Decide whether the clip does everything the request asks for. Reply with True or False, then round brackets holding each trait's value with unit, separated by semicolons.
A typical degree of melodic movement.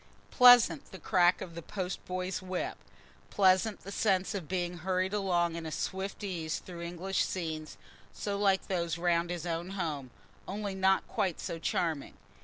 False (2.1 semitones)